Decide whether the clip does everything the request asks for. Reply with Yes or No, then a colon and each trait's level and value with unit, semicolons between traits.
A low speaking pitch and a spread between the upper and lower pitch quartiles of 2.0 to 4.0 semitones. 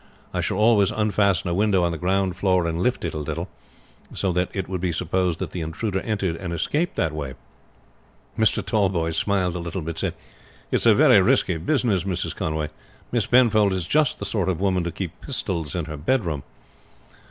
Yes: very low, 90 Hz; average, 3.4 semitones